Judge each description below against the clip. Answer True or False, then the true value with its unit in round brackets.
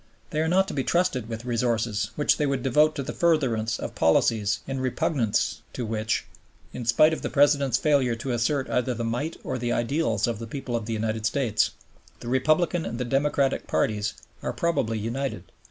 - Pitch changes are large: False (4.1 semitones)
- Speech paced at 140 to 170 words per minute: False (195 wpm)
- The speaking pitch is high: False (125 Hz)